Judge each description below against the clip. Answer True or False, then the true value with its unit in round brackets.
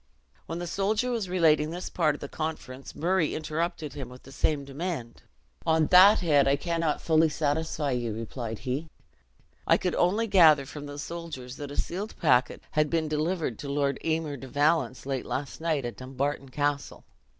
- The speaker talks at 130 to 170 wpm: False (180 wpm)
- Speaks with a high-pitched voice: False (150 Hz)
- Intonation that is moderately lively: True (3.4 semitones)